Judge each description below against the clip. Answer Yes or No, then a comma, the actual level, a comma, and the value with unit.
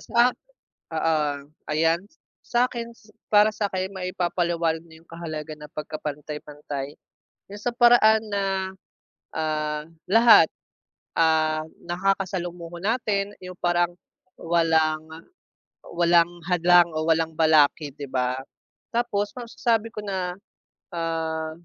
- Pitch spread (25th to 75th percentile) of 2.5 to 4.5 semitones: Yes, average, 3.9 semitones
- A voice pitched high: No, medium, 170 Hz